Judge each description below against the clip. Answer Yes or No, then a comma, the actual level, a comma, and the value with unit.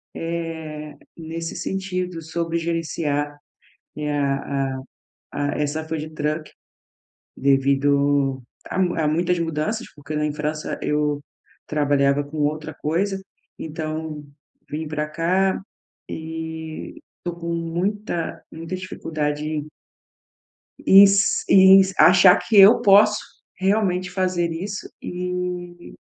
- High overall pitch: No, medium, 160 Hz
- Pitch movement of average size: Yes, average, 3.2 semitones